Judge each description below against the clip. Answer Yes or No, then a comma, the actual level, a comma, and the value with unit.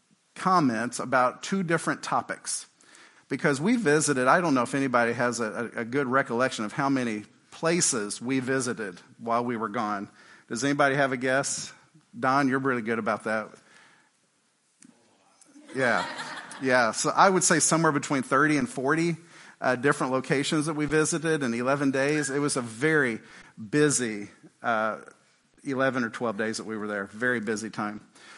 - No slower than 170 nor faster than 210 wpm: No, average, 160 wpm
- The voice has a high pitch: No, low, 135 Hz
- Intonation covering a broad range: No, average, 4.3 semitones